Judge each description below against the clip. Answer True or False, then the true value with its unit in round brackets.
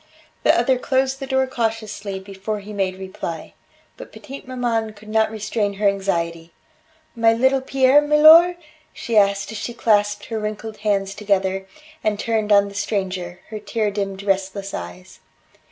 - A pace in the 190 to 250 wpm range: False (155 wpm)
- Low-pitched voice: False (210 Hz)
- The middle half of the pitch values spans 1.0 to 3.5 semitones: True (2.9 semitones)